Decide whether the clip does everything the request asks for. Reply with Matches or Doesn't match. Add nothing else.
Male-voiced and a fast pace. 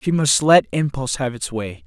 Matches